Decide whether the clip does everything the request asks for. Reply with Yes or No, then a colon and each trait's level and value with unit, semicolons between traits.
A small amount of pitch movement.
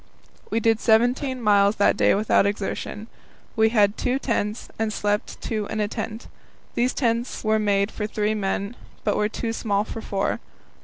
Yes: narrow, 1.8 semitones